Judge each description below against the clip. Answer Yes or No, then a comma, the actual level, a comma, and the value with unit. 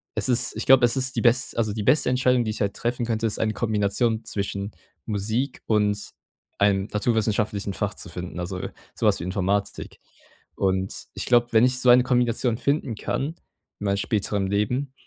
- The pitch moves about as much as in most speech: Yes, average, 3.4 semitones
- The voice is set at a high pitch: No, low, 110 Hz